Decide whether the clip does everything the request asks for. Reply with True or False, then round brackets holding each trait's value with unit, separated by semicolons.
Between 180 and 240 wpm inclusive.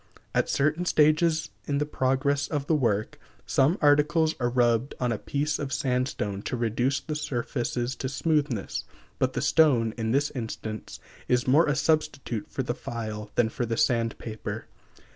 False (165 wpm)